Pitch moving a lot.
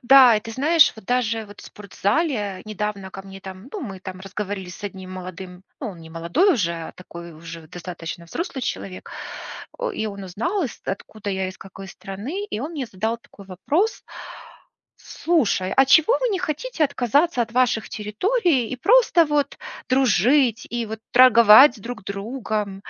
Yes: wide, 6.0 semitones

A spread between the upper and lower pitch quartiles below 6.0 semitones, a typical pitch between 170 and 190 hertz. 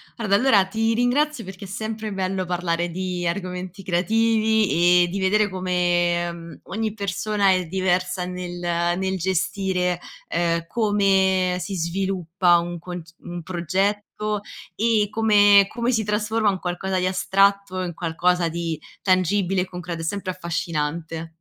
Yes: narrow, 2.6 semitones; medium, 185 Hz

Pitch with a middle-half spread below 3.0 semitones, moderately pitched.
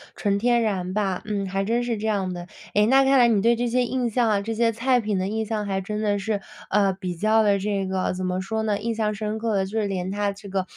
No: narrow, 2.5 semitones; high, 210 Hz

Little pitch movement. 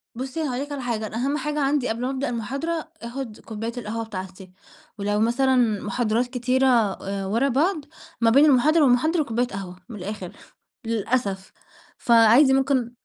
No: average, 3.8 semitones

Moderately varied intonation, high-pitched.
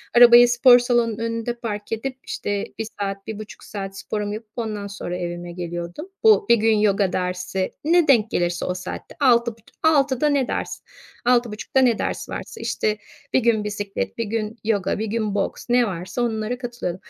Yes: average, 3.3 semitones; high, 220 Hz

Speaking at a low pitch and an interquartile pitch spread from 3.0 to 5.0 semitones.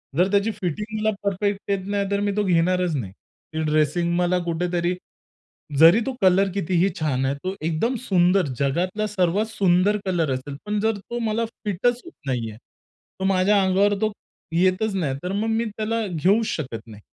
No: medium, 185 Hz; average, 3.7 semitones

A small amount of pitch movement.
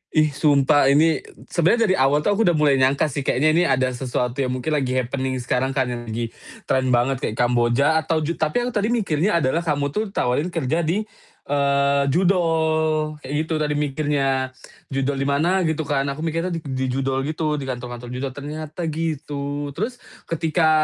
No: average, 3.3 semitones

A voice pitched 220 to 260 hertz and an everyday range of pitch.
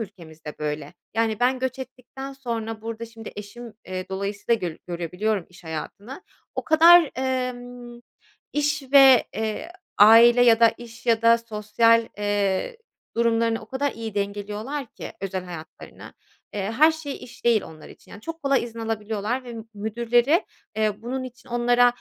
Yes: high, 230 Hz; average, 3.4 semitones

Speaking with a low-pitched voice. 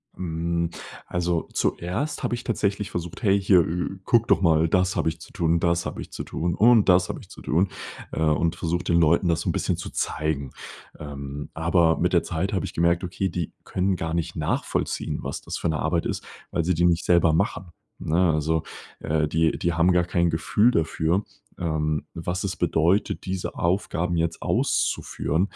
Yes: very low, 85 Hz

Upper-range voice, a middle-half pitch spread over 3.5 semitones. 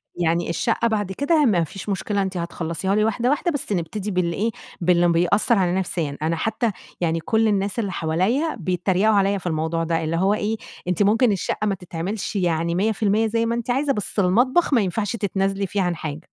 Yes: high, 195 Hz; average, 4.3 semitones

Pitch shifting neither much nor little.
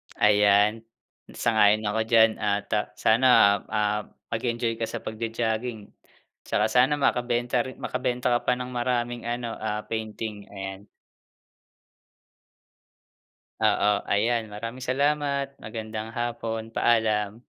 No: narrow, 2.2 semitones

